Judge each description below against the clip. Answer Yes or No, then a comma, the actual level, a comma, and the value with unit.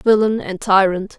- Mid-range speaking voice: No, high, 200 Hz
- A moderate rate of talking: Yes, average, 150 wpm